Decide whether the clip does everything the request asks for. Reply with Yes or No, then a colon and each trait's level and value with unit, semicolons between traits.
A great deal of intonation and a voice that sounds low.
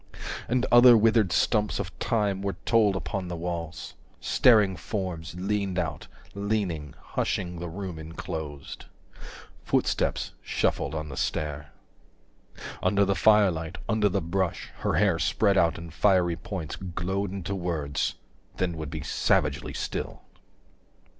No: average, 3.6 semitones; very low, 90 Hz